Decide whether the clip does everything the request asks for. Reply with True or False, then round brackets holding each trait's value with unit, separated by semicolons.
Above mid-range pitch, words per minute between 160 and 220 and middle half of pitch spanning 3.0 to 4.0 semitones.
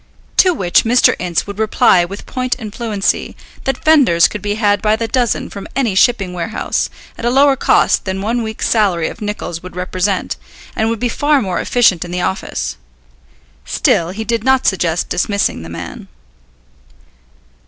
False (205 Hz; 175 wpm; 4.7 semitones)